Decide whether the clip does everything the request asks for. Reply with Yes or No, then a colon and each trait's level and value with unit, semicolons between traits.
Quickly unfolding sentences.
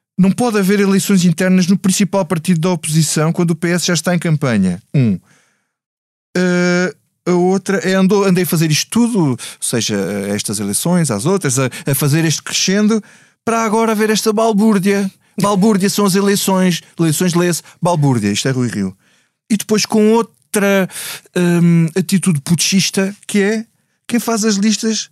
No: average, 160 wpm